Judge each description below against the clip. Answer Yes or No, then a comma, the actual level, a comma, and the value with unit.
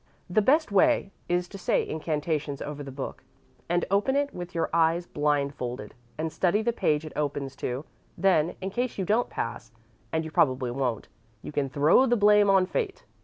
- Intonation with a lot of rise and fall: Yes, wide, 5.8 semitones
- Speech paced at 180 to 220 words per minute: Yes, average, 185 wpm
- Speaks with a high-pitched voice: No, medium, 165 Hz